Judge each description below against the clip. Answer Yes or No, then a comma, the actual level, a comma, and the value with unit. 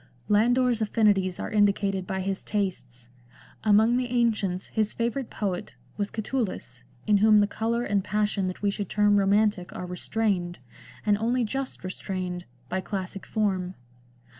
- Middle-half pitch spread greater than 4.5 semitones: No, average, 2.7 semitones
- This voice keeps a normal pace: Yes, average, 155 wpm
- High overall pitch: Yes, high, 205 Hz